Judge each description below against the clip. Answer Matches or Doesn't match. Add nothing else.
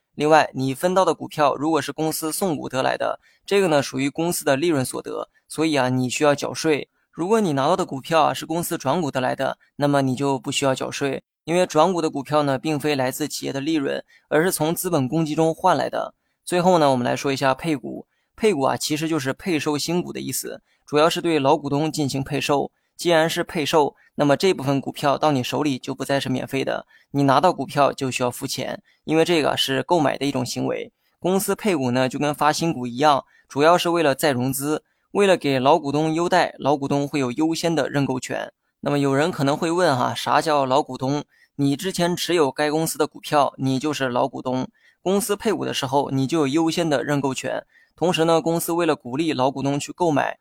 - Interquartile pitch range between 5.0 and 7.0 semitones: Doesn't match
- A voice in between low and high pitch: Matches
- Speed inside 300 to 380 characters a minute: Matches